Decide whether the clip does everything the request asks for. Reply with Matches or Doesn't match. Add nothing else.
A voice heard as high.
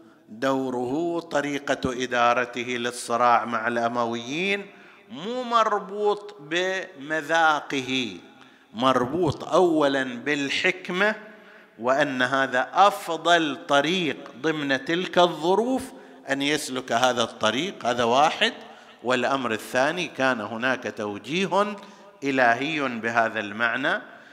Doesn't match